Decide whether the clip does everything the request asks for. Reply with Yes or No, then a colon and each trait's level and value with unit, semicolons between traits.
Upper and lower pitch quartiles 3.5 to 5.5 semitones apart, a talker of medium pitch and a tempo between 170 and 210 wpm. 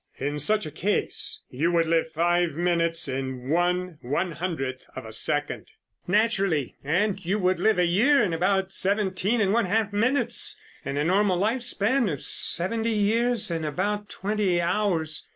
No: average, 4.4 semitones; medium, 180 Hz; average, 160 wpm